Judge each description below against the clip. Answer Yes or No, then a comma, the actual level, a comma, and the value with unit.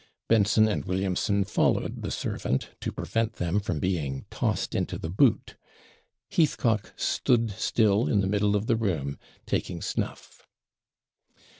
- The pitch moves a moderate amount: Yes, average, 3.1 semitones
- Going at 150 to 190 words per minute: No, slow, 135 wpm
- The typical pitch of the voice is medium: No, low, 100 Hz